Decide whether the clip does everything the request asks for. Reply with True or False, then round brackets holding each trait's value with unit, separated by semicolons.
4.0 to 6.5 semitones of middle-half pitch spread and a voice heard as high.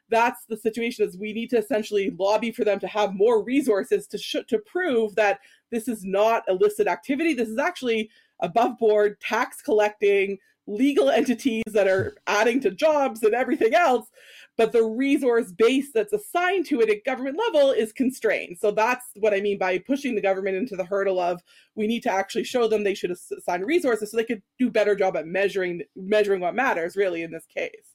True (4.4 semitones; 225 Hz)